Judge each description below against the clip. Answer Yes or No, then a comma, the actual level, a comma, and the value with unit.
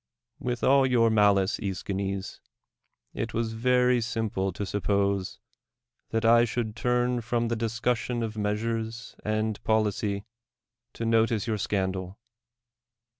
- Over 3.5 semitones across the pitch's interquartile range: No, narrow, 2.5 semitones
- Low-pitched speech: Yes, low, 110 Hz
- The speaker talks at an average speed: No, slow, 125 wpm